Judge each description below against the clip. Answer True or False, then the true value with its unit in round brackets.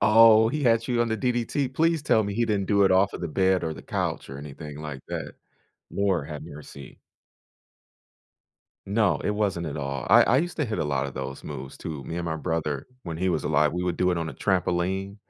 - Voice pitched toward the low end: True (90 Hz)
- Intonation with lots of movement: True (6.2 semitones)